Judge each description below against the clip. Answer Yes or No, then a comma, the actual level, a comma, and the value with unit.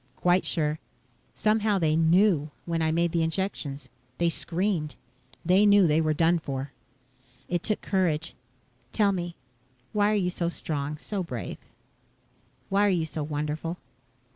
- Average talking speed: Yes, average, 145 wpm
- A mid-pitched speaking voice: Yes, medium, 170 Hz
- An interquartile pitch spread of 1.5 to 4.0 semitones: Yes, average, 3.6 semitones